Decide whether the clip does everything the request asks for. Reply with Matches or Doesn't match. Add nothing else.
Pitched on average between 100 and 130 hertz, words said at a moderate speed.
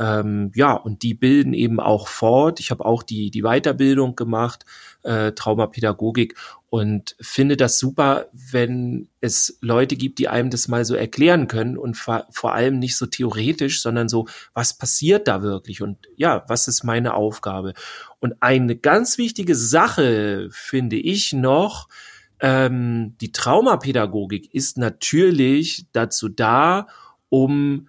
Matches